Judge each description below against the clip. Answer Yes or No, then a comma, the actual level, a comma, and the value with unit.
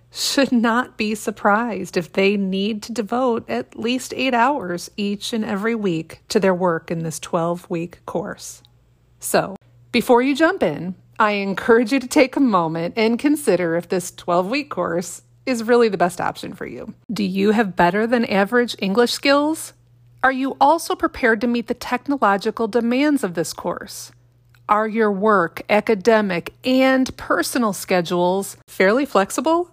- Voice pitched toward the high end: Yes, high, 215 Hz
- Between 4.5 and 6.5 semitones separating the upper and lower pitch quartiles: Yes, wide, 5.5 semitones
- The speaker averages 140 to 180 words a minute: Yes, average, 160 wpm